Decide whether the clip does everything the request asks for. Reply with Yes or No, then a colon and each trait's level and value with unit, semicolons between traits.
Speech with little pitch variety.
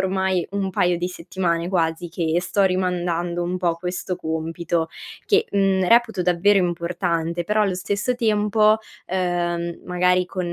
Yes: narrow, 1.9 semitones